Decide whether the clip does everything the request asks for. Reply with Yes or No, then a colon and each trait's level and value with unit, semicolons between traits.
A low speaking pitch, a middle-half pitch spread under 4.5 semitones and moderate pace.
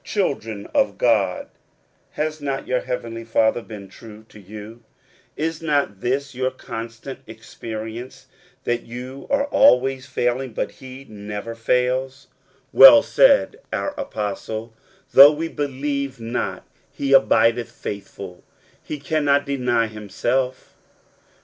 No: low, 125 Hz; average, 3.7 semitones; slow, 125 wpm